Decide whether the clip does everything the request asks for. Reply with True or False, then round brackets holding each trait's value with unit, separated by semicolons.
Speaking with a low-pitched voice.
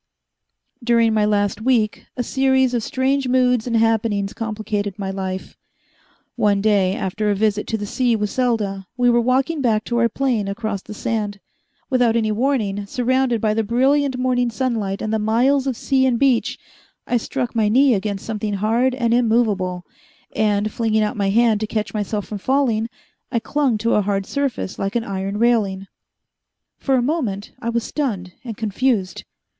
False (225 Hz)